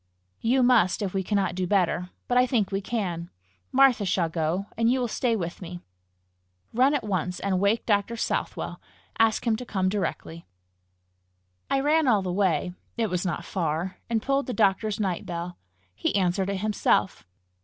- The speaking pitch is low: No, high, 200 Hz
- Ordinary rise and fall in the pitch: Yes, average, 4.3 semitones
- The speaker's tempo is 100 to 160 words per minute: No, average, 175 wpm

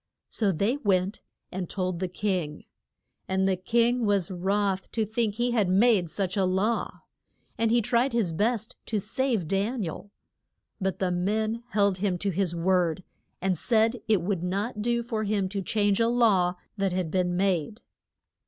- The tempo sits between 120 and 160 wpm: No, average, 175 wpm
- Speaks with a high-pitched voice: Yes, high, 200 Hz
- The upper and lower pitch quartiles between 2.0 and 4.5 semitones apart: Yes, average, 3.4 semitones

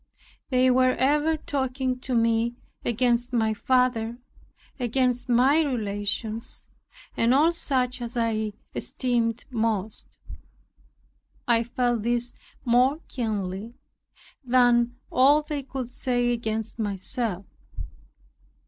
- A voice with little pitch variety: Yes, narrow, 2.1 semitones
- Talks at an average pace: No, slow, 100 wpm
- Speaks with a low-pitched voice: No, high, 240 Hz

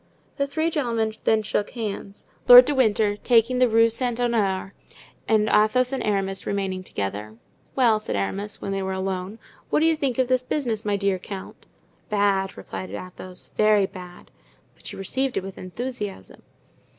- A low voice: No, high, 210 Hz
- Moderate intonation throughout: Yes, average, 4.2 semitones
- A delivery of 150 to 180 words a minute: Yes, average, 170 wpm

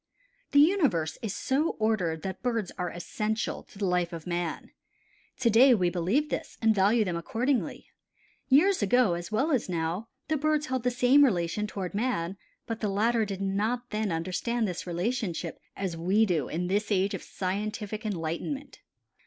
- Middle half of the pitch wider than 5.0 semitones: Yes, wide, 5.4 semitones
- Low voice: No, high, 210 Hz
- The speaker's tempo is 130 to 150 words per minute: No, average, 170 wpm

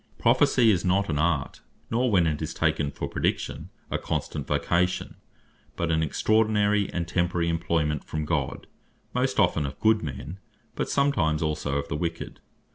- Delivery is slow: No, average, 160 wpm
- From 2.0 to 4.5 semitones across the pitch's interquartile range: No, average, 5.0 semitones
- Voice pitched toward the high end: No, very low, 85 Hz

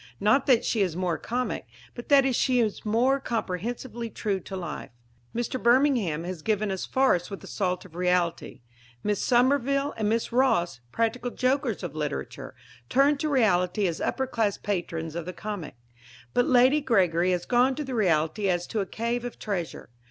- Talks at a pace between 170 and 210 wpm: Yes, average, 175 wpm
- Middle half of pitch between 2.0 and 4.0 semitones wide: No, wide, 5.6 semitones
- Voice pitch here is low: No, high, 215 Hz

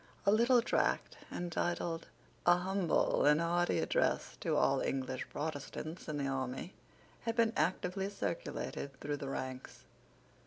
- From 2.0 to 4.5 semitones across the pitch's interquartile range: No, average, 5.2 semitones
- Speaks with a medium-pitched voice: Yes, medium, 170 Hz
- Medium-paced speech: No, slow, 130 wpm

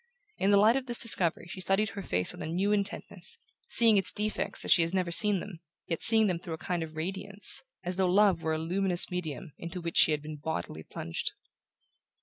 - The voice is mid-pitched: Yes, medium, 180 Hz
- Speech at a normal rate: No, fast, 220 wpm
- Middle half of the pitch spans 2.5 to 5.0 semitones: Yes, average, 3.6 semitones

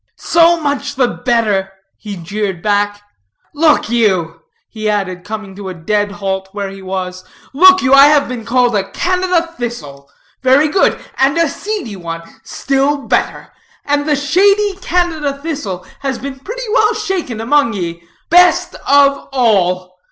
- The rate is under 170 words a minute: Yes, average, 150 wpm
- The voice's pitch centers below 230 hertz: No, high, 245 Hz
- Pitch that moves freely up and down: Yes, wide, 7.4 semitones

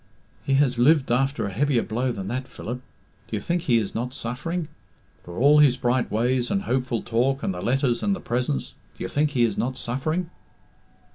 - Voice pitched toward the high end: No, low, 125 Hz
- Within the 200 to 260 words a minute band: Yes, fast, 205 wpm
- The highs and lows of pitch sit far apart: No, average, 3.2 semitones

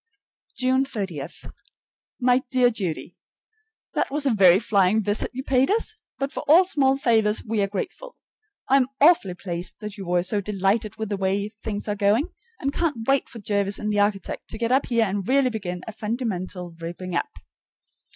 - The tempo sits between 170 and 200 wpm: Yes, average, 190 wpm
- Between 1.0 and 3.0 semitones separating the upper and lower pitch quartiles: No, average, 4.8 semitones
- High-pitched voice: Yes, high, 215 Hz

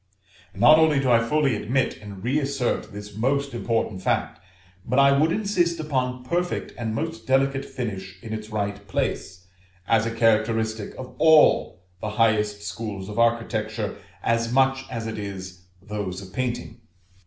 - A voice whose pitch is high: No, low, 115 Hz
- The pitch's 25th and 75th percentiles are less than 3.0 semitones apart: No, average, 4.3 semitones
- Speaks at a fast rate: No, average, 155 wpm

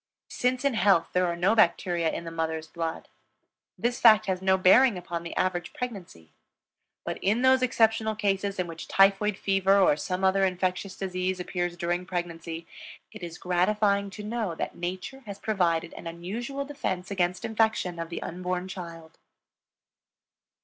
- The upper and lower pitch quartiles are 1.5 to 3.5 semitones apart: Yes, average, 3.2 semitones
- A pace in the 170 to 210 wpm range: No, average, 160 wpm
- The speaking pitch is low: No, medium, 185 Hz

